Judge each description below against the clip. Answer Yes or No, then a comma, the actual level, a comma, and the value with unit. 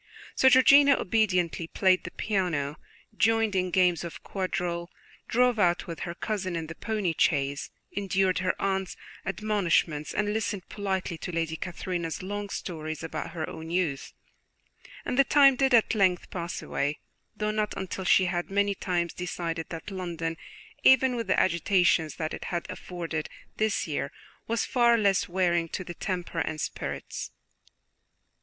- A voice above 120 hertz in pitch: Yes, medium, 185 Hz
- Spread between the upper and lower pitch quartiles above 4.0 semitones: No, average, 3.6 semitones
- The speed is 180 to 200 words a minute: No, average, 155 wpm